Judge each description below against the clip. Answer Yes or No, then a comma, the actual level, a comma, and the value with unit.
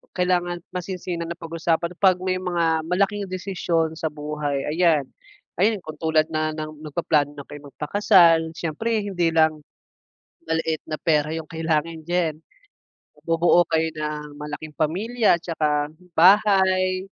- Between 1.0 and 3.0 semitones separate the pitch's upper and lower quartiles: Yes, average, 2.7 semitones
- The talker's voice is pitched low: No, medium, 165 Hz